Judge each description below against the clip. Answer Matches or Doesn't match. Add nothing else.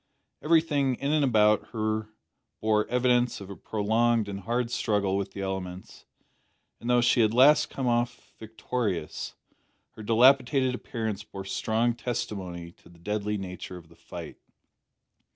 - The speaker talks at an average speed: Matches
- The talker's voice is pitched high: Doesn't match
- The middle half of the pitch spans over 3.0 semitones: Matches